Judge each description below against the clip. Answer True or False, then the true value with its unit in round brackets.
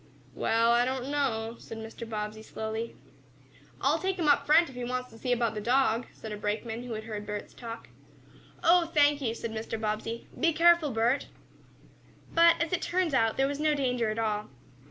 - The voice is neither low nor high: False (240 Hz)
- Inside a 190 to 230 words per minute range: True (195 wpm)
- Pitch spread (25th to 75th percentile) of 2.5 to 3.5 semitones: False (4.5 semitones)